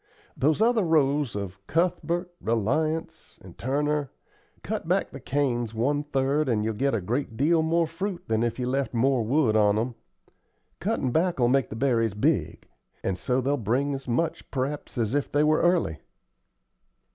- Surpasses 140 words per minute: Yes, average, 170 wpm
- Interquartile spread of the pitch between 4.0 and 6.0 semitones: Yes, average, 4.9 semitones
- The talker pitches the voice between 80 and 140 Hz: Yes, low, 135 Hz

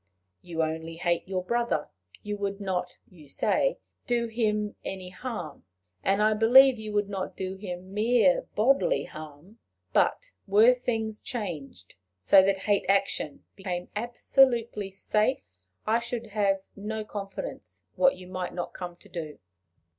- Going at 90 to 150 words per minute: Yes, average, 145 wpm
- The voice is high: Yes, high, 200 Hz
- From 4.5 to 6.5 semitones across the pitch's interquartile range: No, average, 3.7 semitones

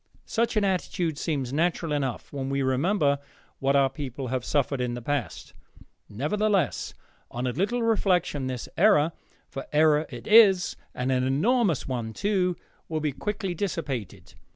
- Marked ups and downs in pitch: Yes, wide, 6.1 semitones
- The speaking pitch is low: No, medium, 150 Hz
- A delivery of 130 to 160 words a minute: Yes, average, 155 wpm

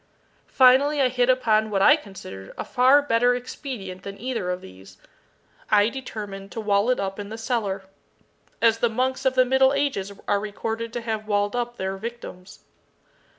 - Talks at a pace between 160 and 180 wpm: Yes, average, 175 wpm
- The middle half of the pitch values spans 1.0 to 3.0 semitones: No, average, 4.1 semitones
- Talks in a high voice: Yes, high, 225 Hz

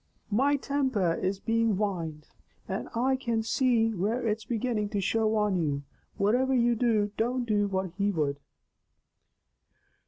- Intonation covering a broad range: No, average, 3.4 semitones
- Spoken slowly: No, average, 145 wpm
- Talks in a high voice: Yes, high, 220 Hz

